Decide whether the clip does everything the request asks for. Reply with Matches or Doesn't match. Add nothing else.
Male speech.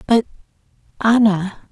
Doesn't match